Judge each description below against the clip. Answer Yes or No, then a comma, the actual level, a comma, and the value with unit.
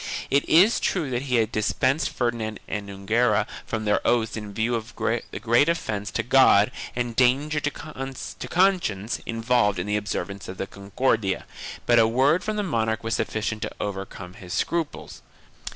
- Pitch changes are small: No, average, 4.3 semitones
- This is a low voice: Yes, low, 115 Hz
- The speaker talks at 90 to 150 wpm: No, average, 170 wpm